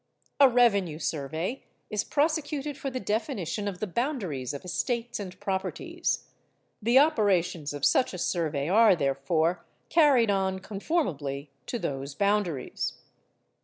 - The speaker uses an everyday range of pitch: No, wide, 7.2 semitones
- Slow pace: Yes, slow, 130 wpm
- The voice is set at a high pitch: Yes, high, 195 Hz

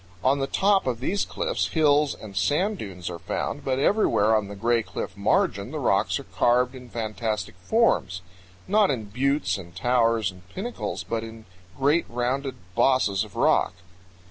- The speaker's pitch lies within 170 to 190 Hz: No, low, 120 Hz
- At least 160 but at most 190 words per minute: Yes, average, 170 wpm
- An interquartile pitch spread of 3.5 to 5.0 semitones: No, wide, 5.4 semitones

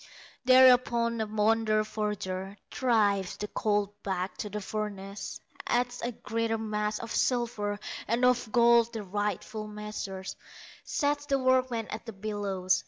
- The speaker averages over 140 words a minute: No, slow, 135 wpm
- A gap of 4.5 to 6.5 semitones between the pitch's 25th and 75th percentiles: No, narrow, 2.5 semitones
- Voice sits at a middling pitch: No, high, 215 Hz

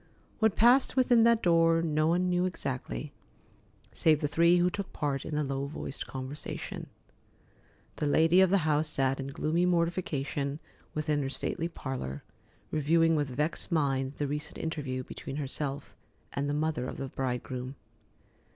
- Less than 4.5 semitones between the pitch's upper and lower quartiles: Yes, average, 3.5 semitones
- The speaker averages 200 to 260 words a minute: No, average, 155 wpm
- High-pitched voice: No, medium, 150 Hz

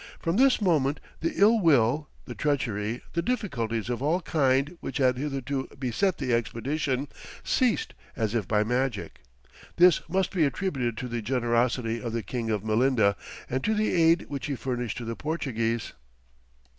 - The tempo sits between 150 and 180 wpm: Yes, average, 165 wpm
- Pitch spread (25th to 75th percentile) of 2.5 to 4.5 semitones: No, average, 5.2 semitones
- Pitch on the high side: No, low, 130 Hz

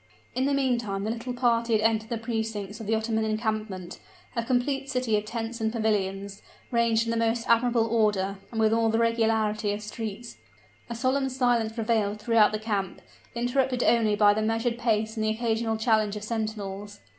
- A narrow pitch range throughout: Yes, narrow, 1.6 semitones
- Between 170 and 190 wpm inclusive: Yes, average, 185 wpm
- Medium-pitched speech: No, high, 225 Hz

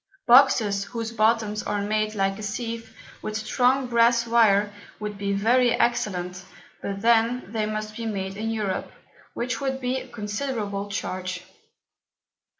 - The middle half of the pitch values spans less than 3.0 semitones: Yes, narrow, 2.6 semitones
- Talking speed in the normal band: Yes, average, 145 wpm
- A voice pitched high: Yes, high, 215 Hz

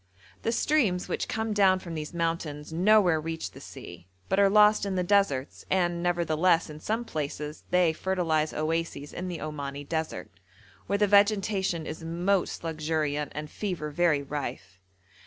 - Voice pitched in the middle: Yes, medium, 170 Hz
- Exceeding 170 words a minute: No, average, 155 wpm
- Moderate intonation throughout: Yes, average, 3.9 semitones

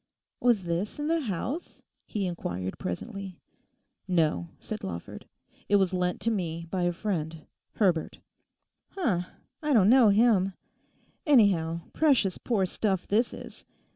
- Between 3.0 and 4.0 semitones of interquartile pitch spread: No, average, 4.9 semitones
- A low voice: No, high, 195 Hz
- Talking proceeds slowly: Yes, slow, 125 wpm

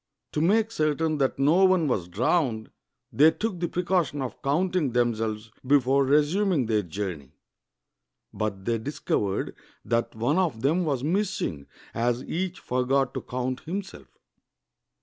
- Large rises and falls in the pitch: Yes, wide, 6.8 semitones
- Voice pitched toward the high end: No, low, 135 Hz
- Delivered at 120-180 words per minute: Yes, average, 140 wpm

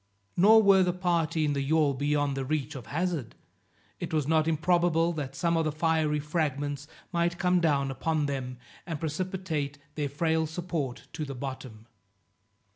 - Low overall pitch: No, medium, 155 Hz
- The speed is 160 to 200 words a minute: Yes, average, 165 wpm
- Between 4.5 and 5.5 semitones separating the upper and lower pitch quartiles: No, average, 3.2 semitones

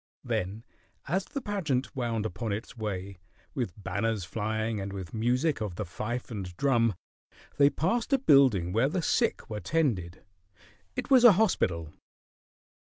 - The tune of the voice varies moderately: No, wide, 6.8 semitones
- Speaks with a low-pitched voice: Yes, low, 115 Hz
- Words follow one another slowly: No, average, 150 wpm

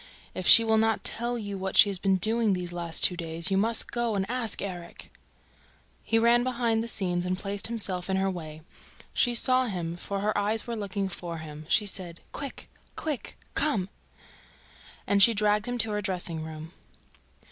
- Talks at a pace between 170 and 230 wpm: Yes, average, 190 wpm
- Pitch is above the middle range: Yes, high, 200 Hz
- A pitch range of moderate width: Yes, average, 4.0 semitones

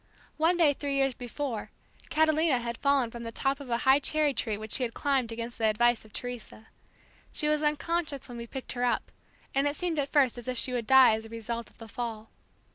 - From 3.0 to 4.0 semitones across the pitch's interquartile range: Yes, average, 3.6 semitones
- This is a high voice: Yes, very high, 250 Hz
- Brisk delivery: Yes, fast, 230 wpm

